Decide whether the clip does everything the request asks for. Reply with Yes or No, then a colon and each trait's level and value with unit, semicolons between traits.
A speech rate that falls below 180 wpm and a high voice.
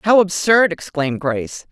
No: average, 140 wpm; medium, 170 Hz